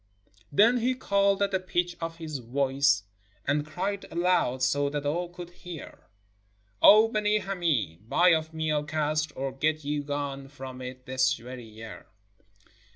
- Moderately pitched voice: Yes, medium, 150 Hz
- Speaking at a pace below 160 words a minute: No, average, 165 wpm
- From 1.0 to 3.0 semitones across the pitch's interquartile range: No, average, 5.2 semitones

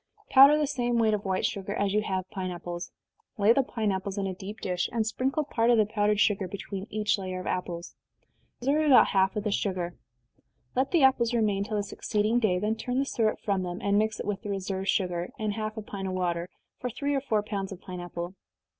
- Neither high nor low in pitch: No, high, 205 Hz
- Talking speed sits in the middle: No, fast, 235 wpm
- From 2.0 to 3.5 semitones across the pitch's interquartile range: Yes, average, 3.0 semitones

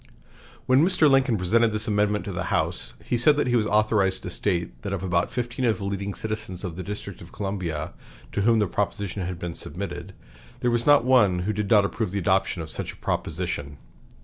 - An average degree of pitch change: Yes, average, 4.0 semitones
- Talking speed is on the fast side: Yes, fast, 215 wpm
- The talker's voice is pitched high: No, low, 100 Hz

